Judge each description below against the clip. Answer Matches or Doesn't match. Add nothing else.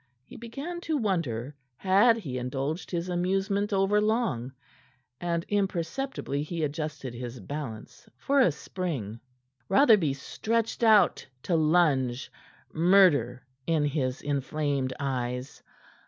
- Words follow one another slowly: Matches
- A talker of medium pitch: Matches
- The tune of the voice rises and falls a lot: Matches